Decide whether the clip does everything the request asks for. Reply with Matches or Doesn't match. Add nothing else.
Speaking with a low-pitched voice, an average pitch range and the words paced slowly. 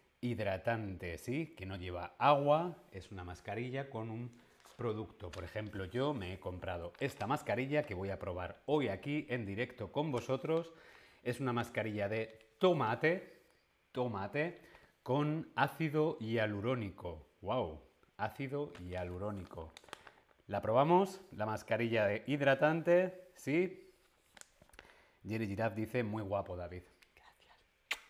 Doesn't match